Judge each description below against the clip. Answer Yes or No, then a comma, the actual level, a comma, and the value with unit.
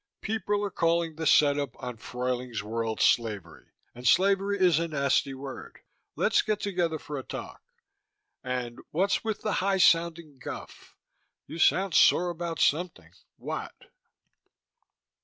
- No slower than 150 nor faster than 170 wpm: No, slow, 135 wpm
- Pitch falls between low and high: Yes, medium, 160 Hz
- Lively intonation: Yes, wide, 6.4 semitones